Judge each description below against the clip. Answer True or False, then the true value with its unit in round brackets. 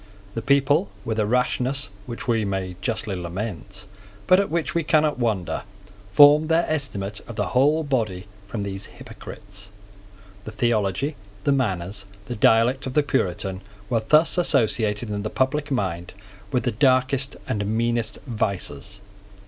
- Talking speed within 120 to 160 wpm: True (150 wpm)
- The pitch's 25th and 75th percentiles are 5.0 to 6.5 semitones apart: True (5.4 semitones)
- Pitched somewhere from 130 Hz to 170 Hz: False (115 Hz)